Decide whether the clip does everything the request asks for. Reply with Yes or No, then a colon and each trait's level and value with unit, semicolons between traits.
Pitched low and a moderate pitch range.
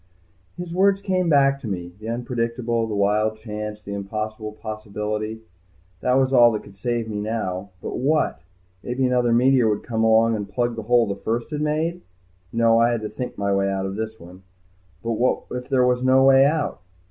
Yes: low, 115 Hz; average, 3.2 semitones